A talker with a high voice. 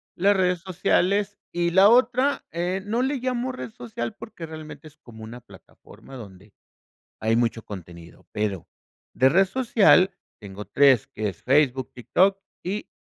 No: medium, 160 Hz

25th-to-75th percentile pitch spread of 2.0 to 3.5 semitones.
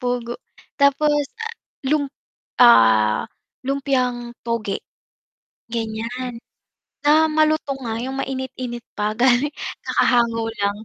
Yes: average, 3.2 semitones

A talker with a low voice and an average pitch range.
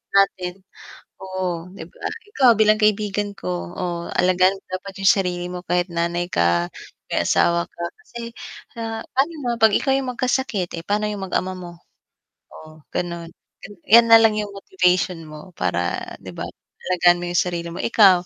No: medium, 185 Hz; average, 3.5 semitones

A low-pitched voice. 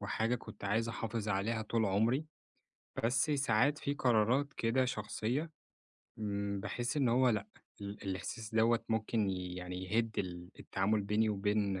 Yes: low, 110 Hz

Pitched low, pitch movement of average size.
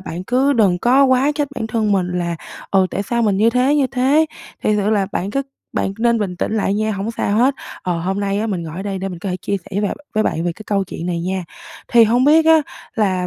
No: high, 205 Hz; average, 4.3 semitones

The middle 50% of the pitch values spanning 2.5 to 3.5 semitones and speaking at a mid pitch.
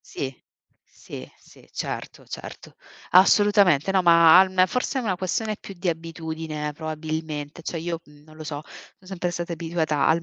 Yes: average, 2.8 semitones; medium, 165 Hz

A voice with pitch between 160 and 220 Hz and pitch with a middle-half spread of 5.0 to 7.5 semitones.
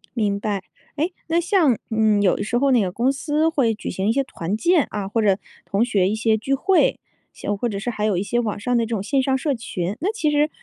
No: high, 230 Hz; average, 5.3 semitones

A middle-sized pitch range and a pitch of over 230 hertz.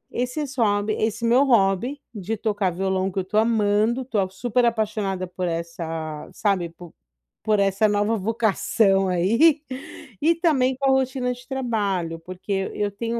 No: average, 4.1 semitones; high, 210 Hz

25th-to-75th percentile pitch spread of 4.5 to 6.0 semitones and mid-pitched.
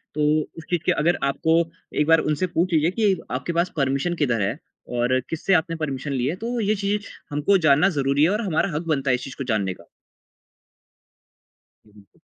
Yes: average, 4.8 semitones; medium, 155 Hz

